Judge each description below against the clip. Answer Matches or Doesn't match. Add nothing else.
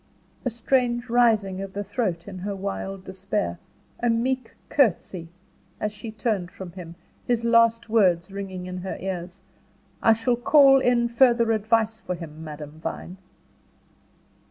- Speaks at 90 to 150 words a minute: Matches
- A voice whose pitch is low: Doesn't match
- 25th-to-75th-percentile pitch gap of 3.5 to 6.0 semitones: Matches